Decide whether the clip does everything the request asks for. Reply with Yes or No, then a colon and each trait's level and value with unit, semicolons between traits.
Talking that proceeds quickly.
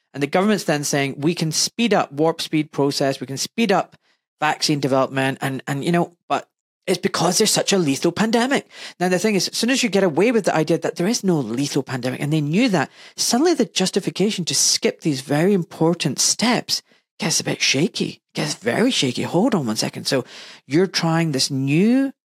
Yes: fast, 210 wpm